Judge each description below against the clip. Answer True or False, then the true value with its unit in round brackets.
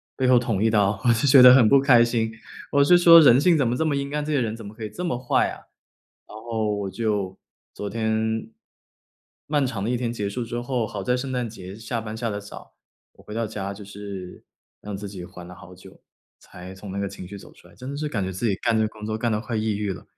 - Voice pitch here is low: True (110 Hz)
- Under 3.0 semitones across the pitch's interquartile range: False (3.5 semitones)